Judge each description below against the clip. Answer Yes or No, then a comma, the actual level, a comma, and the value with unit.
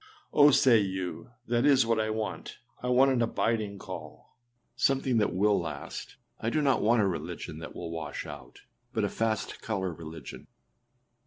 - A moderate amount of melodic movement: Yes, average, 4.8 semitones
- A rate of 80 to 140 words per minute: No, average, 175 wpm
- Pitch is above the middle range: No, low, 110 Hz